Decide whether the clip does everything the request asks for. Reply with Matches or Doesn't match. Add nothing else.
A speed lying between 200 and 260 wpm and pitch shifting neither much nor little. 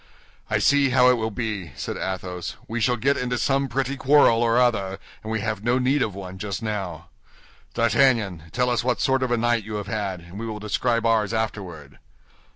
Matches